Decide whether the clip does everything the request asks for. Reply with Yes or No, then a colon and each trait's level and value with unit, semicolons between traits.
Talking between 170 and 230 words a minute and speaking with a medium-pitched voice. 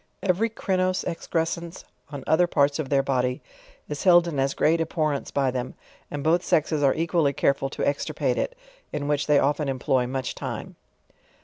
Yes: average, 175 wpm; medium, 150 Hz